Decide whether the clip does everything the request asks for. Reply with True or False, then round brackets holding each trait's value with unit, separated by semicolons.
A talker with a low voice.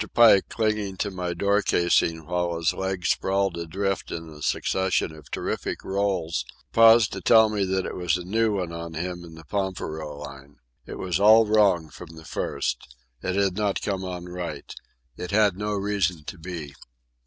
True (90 Hz)